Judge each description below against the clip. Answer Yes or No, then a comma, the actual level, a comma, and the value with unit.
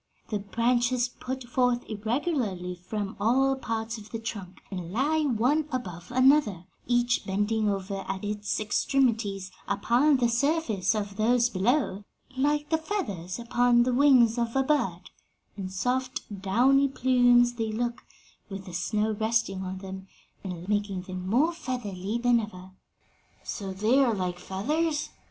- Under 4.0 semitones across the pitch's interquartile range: No, average, 4.6 semitones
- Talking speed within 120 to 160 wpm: Yes, average, 145 wpm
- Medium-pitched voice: No, high, 225 Hz